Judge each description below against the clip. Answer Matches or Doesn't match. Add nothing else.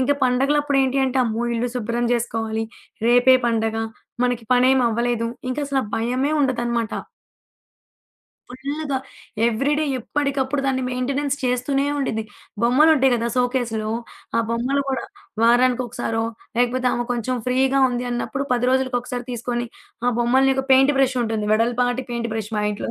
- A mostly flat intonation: Matches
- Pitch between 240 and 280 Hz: Matches